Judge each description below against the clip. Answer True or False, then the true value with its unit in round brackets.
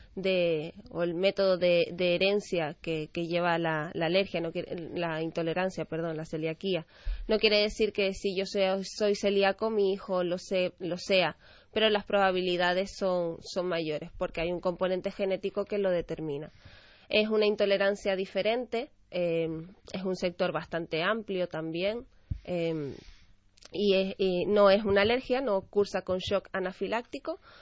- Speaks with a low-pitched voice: False (185 Hz)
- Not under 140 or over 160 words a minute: True (155 wpm)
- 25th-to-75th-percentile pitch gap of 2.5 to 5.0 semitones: True (2.9 semitones)